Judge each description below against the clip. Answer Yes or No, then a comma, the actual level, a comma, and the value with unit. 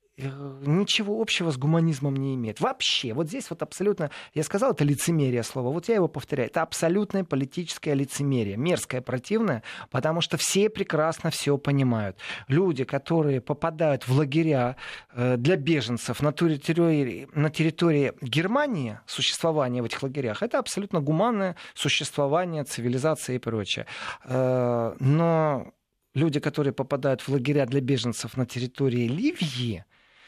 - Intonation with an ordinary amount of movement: Yes, average, 4.2 semitones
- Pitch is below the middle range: No, medium, 145 Hz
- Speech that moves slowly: No, average, 130 wpm